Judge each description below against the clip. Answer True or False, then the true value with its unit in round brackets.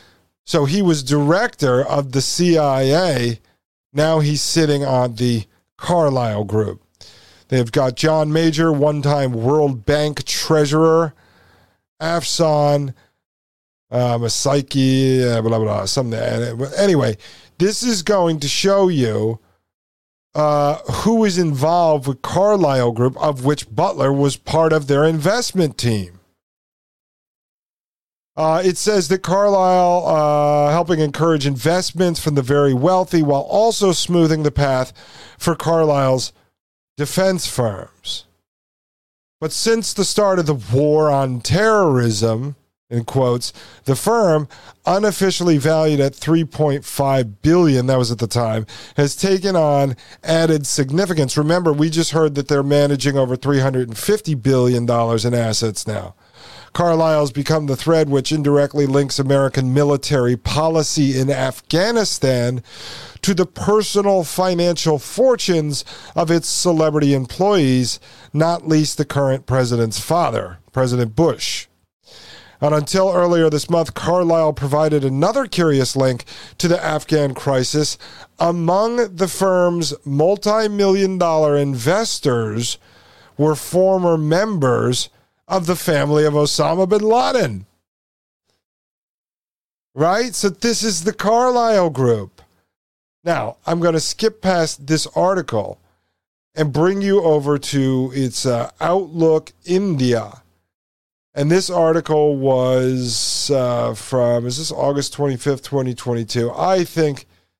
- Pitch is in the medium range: True (145 Hz)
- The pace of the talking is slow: True (120 wpm)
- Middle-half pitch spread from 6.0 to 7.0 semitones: False (5.1 semitones)